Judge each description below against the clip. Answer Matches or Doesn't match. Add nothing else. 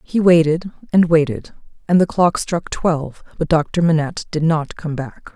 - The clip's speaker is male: Doesn't match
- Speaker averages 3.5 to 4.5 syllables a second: Doesn't match